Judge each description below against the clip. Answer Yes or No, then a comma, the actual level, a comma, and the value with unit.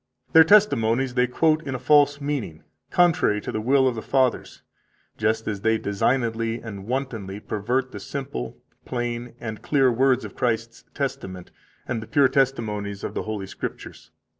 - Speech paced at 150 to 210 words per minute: Yes, average, 165 wpm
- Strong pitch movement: No, average, 3.7 semitones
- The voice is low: Yes, low, 120 Hz